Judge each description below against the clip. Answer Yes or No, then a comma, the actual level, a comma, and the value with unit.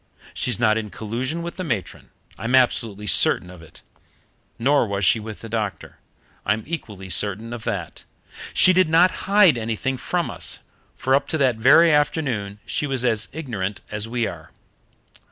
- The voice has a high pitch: No, low, 115 Hz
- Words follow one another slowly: No, average, 170 wpm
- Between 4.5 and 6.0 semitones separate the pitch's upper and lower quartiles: Yes, wide, 5.6 semitones